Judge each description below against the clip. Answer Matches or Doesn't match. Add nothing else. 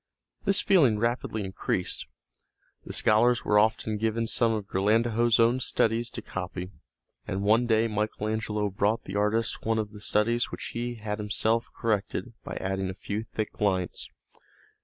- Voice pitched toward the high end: Doesn't match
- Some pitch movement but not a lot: Doesn't match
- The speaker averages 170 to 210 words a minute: Doesn't match